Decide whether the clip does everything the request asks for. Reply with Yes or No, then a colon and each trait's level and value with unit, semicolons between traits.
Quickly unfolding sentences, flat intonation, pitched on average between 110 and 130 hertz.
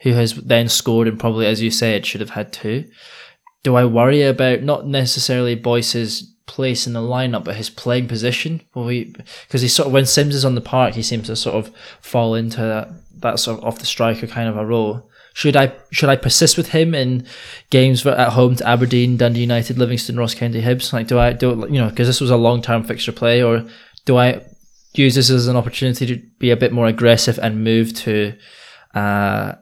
Yes: fast, 225 wpm; narrow, 2.0 semitones; low, 120 Hz